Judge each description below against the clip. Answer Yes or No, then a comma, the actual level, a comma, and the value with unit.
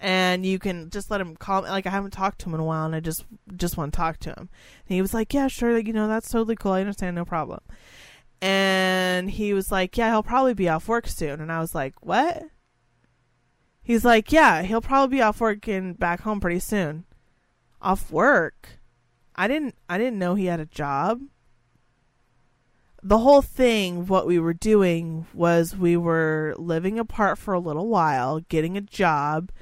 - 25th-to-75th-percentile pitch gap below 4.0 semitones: No, average, 4.9 semitones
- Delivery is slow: No, fast, 205 wpm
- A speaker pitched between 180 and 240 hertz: Yes, medium, 185 Hz